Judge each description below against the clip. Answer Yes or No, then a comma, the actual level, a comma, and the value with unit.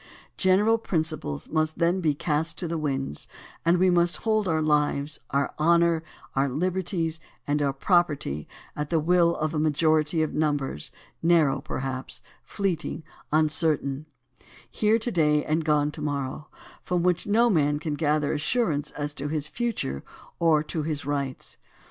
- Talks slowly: No, average, 160 wpm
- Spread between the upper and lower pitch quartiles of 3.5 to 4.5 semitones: No, average, 2.8 semitones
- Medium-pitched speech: Yes, medium, 155 Hz